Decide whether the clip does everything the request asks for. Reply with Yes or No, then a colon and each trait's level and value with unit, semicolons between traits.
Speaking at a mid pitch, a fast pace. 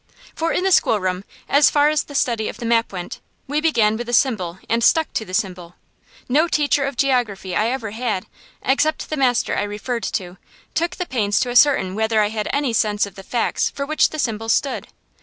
No: high, 235 Hz; fast, 215 wpm